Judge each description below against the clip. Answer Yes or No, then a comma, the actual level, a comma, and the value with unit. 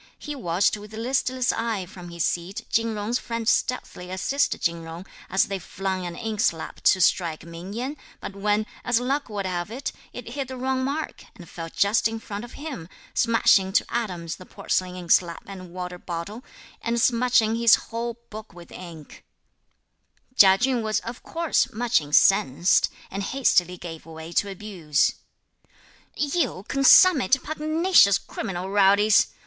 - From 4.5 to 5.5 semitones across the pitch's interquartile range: Yes, average, 5.2 semitones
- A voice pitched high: Yes, high, 205 Hz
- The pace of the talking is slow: No, average, 155 wpm